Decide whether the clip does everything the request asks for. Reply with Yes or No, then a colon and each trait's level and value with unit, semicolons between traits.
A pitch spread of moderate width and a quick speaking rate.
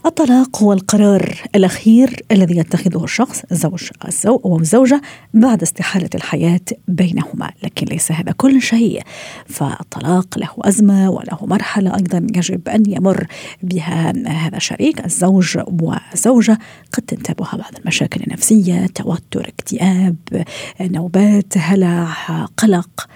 No: average, 3.8 semitones; average, 110 wpm